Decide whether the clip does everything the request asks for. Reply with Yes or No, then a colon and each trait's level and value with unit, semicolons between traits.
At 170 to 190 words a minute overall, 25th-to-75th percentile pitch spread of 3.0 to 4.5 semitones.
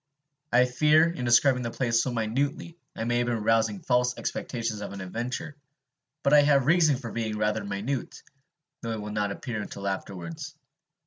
Yes: average, 185 wpm; average, 3.9 semitones